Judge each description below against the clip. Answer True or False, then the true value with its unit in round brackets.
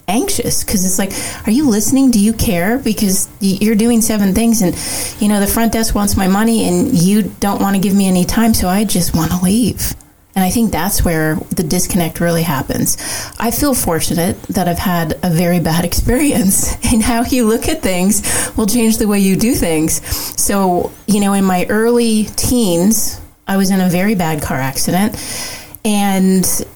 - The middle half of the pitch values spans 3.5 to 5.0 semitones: True (3.8 semitones)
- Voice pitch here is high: True (205 Hz)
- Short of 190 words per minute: False (195 wpm)